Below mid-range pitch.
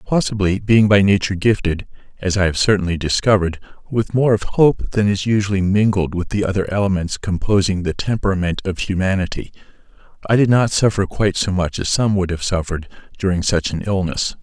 Yes: very low, 95 Hz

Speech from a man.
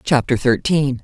No: female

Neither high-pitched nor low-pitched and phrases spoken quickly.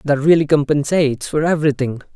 No: medium, 145 Hz; average, 140 wpm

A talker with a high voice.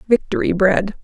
Yes: high, 200 Hz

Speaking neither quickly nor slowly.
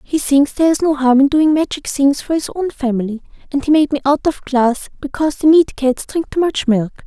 No: fast, 240 wpm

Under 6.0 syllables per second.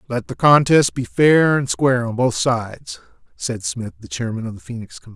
Yes: 5.4 syllables/s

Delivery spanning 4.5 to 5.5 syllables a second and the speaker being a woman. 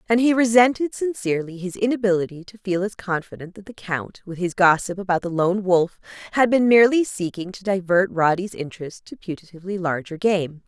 No: 5.7 syllables/s; female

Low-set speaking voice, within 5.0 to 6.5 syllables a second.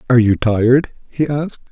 Yes: low, 125 Hz; 6.0 syllables/s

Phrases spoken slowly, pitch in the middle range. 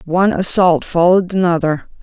Yes: slow, 120 wpm; medium, 175 Hz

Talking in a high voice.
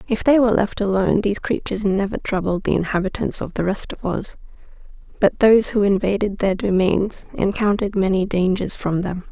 Yes: high, 200 Hz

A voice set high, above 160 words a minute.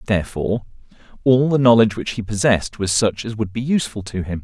No: low, 110 Hz; fast, 205 wpm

